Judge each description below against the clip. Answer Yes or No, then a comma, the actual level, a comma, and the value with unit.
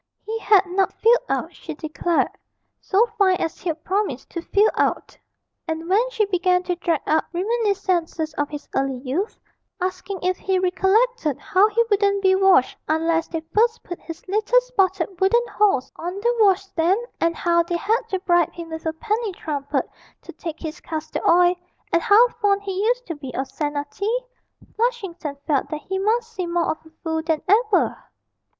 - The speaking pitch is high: Yes, very high, 370 Hz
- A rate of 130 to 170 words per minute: No, average, 180 wpm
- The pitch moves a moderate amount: Yes, average, 4.1 semitones